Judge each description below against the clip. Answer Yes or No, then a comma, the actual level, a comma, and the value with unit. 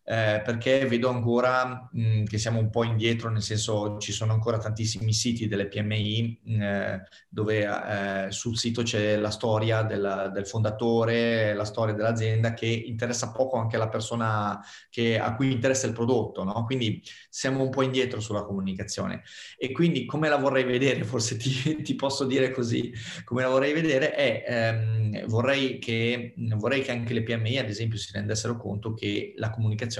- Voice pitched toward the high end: No, low, 115 Hz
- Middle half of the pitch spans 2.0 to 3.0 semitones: Yes, narrow, 2.6 semitones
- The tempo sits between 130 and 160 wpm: No, fast, 170 wpm